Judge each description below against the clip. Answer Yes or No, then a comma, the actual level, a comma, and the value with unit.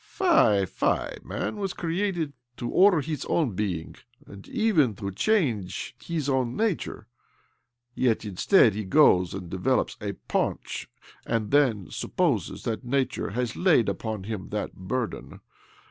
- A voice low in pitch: Yes, low, 120 Hz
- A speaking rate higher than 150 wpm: No, average, 140 wpm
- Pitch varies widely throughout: Yes, wide, 8.0 semitones